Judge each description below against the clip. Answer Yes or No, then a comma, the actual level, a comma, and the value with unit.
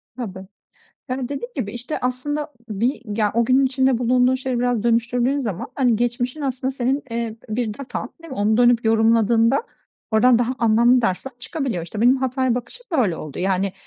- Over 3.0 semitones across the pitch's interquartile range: No, average, 2.7 semitones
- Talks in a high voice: Yes, high, 245 Hz